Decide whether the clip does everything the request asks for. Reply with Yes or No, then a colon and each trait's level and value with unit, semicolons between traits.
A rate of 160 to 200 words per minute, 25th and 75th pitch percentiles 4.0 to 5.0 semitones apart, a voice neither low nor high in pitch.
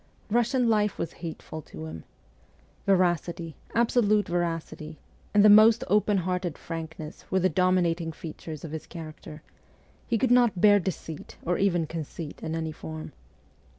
No: average, 145 wpm; average, 4.4 semitones; medium, 175 Hz